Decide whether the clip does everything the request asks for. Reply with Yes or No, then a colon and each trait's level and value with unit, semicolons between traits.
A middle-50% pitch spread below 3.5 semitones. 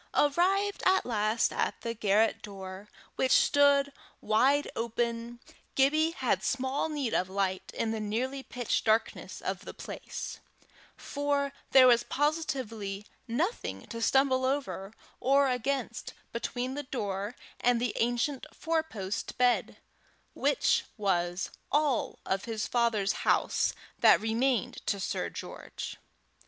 No: average, 4.5 semitones